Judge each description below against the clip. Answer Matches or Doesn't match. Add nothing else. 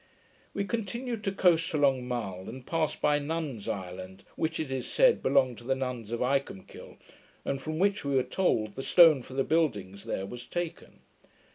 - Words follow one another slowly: Doesn't match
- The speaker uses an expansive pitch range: Matches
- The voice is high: Doesn't match